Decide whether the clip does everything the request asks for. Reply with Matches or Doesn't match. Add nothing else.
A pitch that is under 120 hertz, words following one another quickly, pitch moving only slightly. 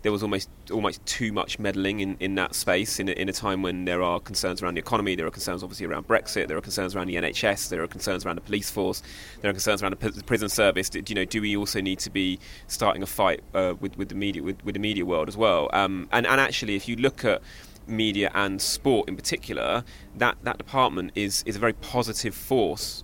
Matches